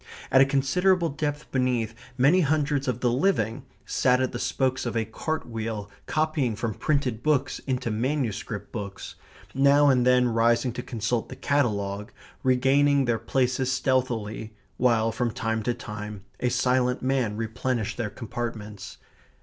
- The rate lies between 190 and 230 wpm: No, average, 150 wpm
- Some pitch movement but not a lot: Yes, average, 3.3 semitones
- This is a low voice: Yes, low, 125 Hz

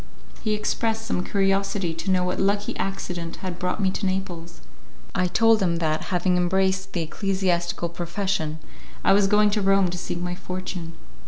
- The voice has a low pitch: No, medium, 185 Hz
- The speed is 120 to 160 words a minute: No, average, 170 wpm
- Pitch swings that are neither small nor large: No, narrow, 2.1 semitones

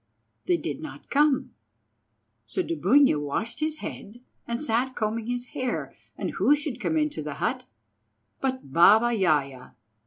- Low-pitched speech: No, high, 245 Hz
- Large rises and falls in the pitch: Yes, wide, 5.9 semitones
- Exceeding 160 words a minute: No, average, 145 wpm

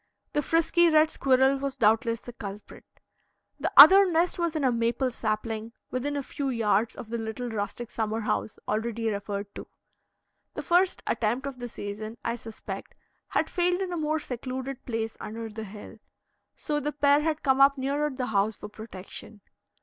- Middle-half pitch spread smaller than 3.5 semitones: No, average, 4.7 semitones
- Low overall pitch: No, high, 245 Hz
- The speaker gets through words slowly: No, average, 175 wpm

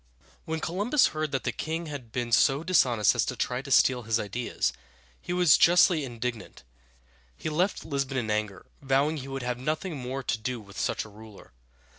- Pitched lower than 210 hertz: Yes, low, 135 Hz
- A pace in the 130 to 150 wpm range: No, average, 190 wpm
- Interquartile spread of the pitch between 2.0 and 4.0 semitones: No, average, 4.9 semitones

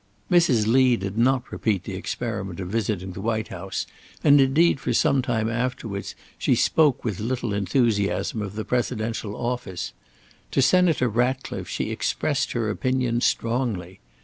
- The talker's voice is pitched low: Yes, low, 115 Hz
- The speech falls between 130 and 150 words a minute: Yes, average, 145 wpm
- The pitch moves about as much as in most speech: Yes, average, 3.8 semitones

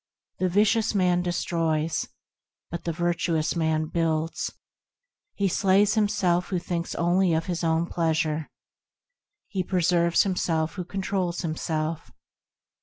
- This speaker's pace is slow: Yes, slow, 115 wpm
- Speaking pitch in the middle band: Yes, medium, 175 Hz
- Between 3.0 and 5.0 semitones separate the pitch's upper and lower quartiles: No, narrow, 2.4 semitones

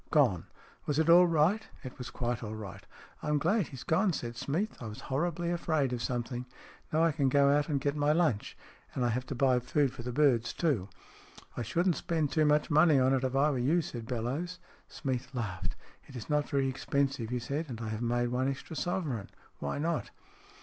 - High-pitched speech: No, low, 135 Hz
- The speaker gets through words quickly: Yes, fast, 230 wpm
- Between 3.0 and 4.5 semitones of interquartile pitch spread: Yes, average, 4.2 semitones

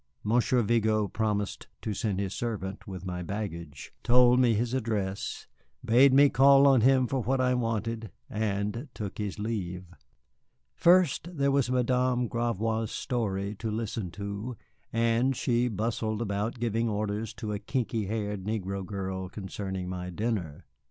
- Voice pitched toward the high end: No, low, 110 Hz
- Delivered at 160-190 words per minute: No, average, 145 wpm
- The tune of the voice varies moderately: Yes, average, 3.4 semitones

